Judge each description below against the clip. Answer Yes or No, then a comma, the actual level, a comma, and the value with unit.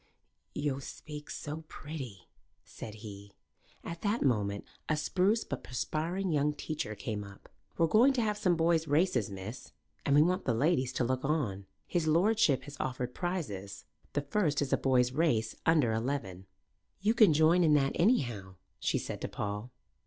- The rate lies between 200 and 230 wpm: No, average, 165 wpm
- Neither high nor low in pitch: Yes, medium, 145 Hz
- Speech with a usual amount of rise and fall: No, wide, 6.8 semitones